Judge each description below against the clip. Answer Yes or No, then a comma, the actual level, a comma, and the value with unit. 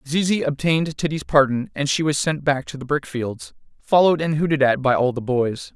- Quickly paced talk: Yes, fast, 220 wpm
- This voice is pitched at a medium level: Yes, medium, 145 Hz